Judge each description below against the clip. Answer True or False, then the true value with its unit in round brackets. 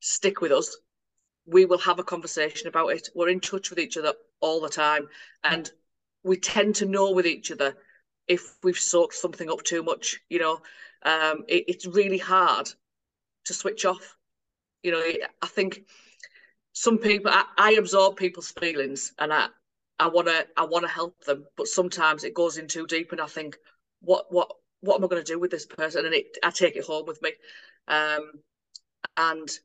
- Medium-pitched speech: True (175 Hz)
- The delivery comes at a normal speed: True (190 wpm)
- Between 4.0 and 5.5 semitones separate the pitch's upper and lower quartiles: False (3.0 semitones)